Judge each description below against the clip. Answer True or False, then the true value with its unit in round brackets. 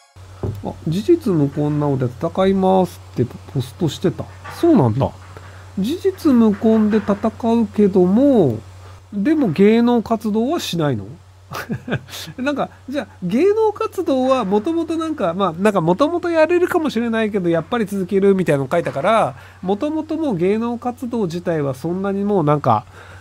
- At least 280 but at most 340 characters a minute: True (320 characters per minute)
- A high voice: True (200 Hz)